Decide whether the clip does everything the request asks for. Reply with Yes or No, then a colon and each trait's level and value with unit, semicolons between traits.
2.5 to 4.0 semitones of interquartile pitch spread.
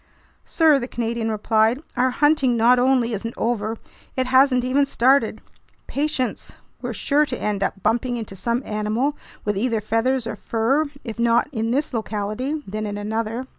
Yes: average, 3.0 semitones